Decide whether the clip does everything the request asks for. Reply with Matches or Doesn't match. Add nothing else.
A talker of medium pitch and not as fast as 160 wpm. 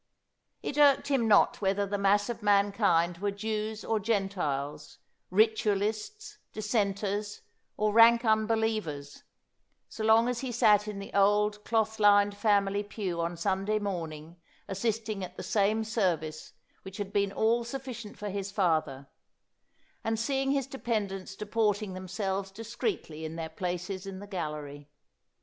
Doesn't match